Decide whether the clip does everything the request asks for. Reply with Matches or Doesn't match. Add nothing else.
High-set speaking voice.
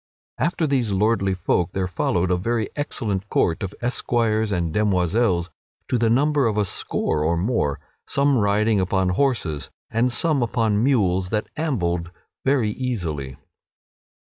Doesn't match